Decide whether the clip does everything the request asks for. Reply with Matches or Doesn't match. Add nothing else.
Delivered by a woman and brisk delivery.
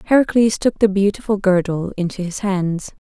Doesn't match